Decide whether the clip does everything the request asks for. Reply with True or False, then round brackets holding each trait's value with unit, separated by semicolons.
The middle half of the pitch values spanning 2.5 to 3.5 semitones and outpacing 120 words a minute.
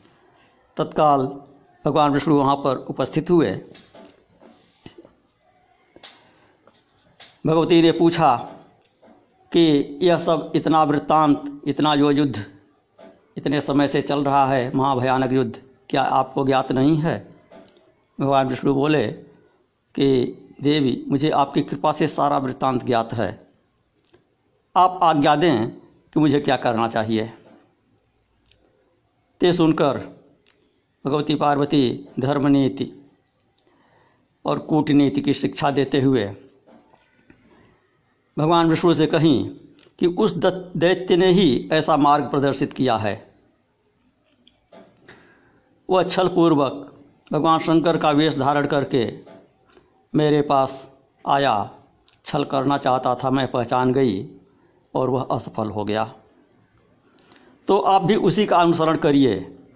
False (3.0 semitones; 110 wpm)